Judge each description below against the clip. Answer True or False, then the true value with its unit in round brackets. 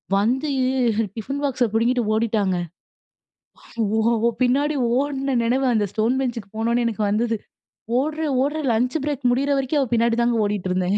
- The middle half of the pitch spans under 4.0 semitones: True (3.6 semitones)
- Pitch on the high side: True (240 Hz)